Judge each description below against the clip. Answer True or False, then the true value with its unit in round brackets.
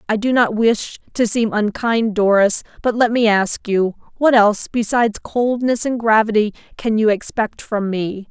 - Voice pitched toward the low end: False (220 Hz)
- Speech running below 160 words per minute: False (165 wpm)